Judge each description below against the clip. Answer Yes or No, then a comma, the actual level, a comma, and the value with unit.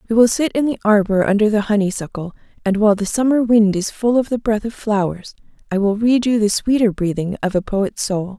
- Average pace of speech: No, fast, 230 wpm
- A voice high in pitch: Yes, high, 210 Hz